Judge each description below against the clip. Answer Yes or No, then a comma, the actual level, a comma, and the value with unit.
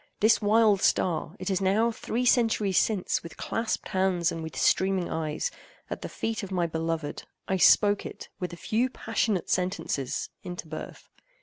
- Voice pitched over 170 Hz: Yes, high, 190 Hz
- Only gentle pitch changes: No, average, 4.2 semitones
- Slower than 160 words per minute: Yes, average, 145 wpm